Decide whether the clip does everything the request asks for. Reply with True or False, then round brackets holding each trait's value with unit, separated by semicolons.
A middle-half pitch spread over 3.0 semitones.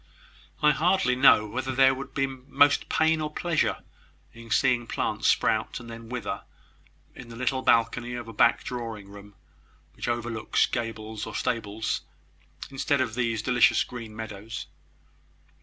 False (2.7 semitones)